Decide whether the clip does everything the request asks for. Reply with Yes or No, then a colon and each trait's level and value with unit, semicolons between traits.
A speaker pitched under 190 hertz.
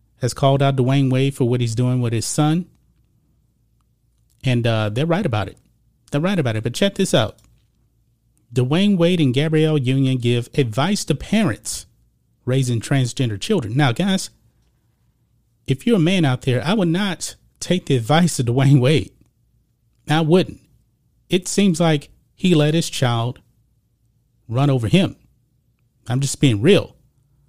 Yes: low, 135 Hz